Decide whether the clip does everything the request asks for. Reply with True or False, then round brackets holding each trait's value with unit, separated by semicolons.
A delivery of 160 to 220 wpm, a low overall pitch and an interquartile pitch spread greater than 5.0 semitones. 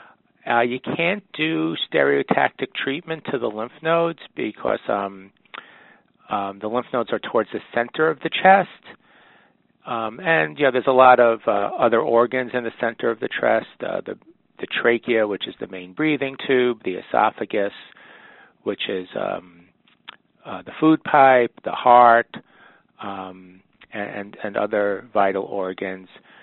False (150 wpm; 120 Hz; 5.6 semitones)